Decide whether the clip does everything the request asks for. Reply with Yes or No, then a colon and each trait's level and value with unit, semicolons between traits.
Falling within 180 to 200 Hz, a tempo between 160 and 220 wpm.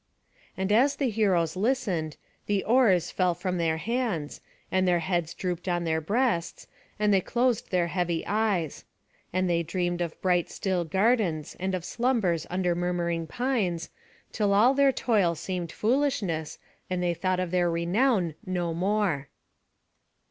No: medium, 185 Hz; average, 150 wpm